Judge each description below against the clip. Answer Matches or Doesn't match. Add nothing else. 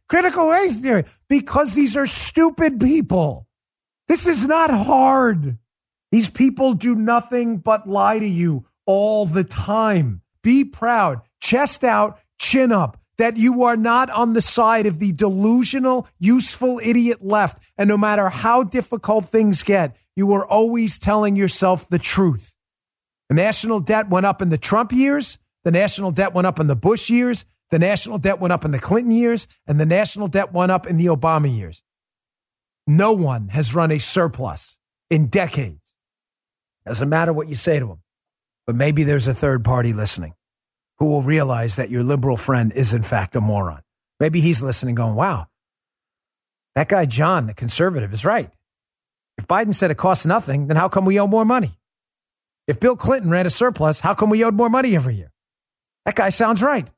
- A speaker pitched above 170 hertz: Matches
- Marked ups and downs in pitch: Matches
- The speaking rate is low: Doesn't match